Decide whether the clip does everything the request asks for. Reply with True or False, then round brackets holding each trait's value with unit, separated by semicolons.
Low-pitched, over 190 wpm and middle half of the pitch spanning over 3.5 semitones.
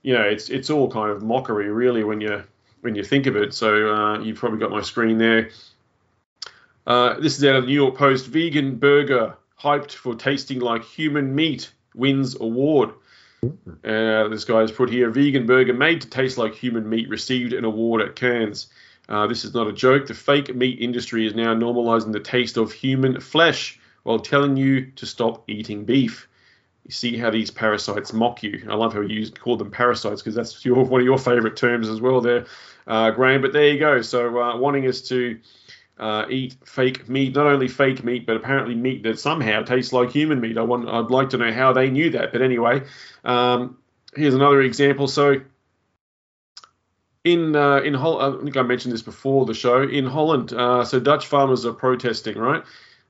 False (125 Hz; 200 wpm; 3.0 semitones)